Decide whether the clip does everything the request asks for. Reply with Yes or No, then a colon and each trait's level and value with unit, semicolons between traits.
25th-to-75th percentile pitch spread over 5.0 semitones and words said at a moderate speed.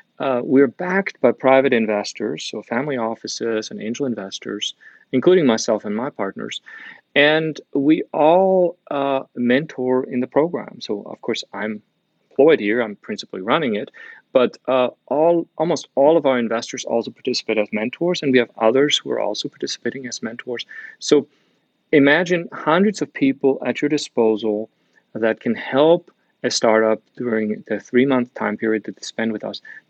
Yes: wide, 5.4 semitones; average, 160 wpm